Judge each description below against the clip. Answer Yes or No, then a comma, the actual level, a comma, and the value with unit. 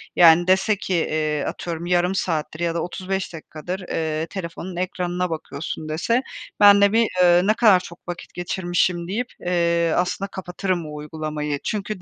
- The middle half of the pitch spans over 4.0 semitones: No, narrow, 2.6 semitones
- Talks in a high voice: No, medium, 175 Hz